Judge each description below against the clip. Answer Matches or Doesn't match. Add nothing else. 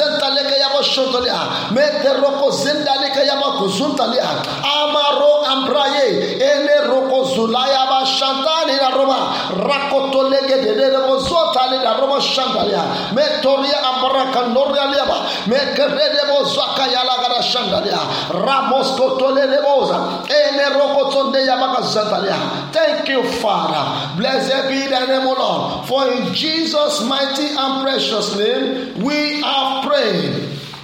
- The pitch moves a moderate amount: Doesn't match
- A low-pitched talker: Doesn't match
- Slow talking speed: Matches